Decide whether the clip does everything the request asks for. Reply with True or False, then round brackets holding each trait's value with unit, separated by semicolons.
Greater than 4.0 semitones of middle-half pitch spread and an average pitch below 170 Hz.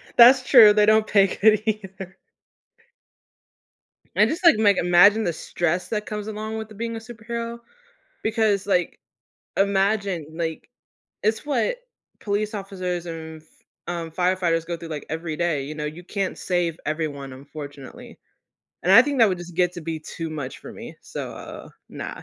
False (4.7 semitones; 190 Hz)